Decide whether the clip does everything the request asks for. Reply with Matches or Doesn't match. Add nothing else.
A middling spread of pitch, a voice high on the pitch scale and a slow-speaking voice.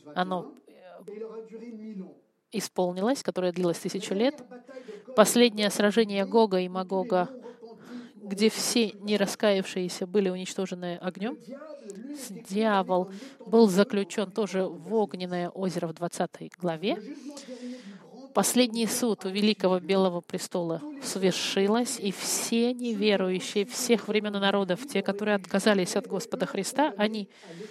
Matches